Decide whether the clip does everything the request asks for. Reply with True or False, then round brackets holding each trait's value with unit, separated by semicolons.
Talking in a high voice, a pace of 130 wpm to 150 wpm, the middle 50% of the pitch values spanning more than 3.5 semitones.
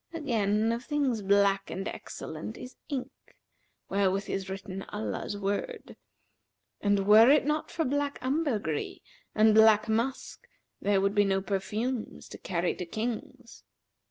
True (215 Hz; 135 wpm; 4.4 semitones)